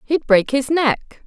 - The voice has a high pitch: Yes, very high, 265 Hz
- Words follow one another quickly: No, average, 190 wpm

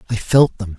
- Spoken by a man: Yes, male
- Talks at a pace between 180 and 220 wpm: No, fast, 230 wpm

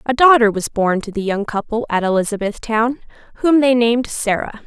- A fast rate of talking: No, average, 180 wpm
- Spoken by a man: No, female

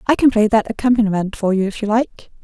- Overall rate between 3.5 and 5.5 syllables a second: No, 6.4 syllables/s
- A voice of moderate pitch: No, high, 220 Hz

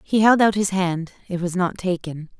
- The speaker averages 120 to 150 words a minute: No, fast, 225 wpm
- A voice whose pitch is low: No, medium, 185 Hz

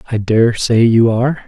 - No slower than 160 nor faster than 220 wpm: Yes, fast, 205 wpm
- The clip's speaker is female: No, male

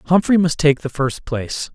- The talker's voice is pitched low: No, medium, 155 Hz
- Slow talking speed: No, fast, 205 wpm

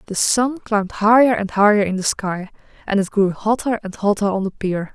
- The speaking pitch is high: Yes, high, 205 Hz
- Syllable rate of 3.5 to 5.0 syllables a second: No, 5.3 syllables/s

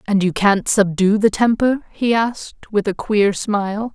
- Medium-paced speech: Yes, average, 180 wpm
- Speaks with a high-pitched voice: Yes, high, 210 Hz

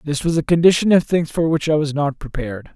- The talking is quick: Yes, fast, 260 wpm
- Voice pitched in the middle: Yes, medium, 155 Hz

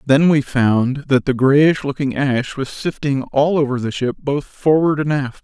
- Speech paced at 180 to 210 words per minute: Yes, average, 200 wpm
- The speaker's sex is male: Yes, male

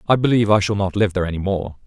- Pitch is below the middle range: Yes, low, 100 Hz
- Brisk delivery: Yes, fast, 290 wpm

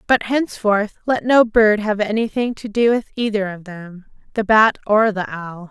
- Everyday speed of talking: Yes, average, 190 wpm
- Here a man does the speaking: No, female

